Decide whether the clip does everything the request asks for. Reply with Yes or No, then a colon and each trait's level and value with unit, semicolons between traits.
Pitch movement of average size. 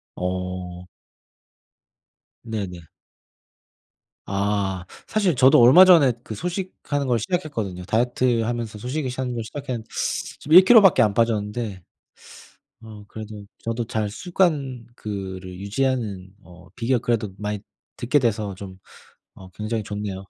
Yes: average, 4.6 semitones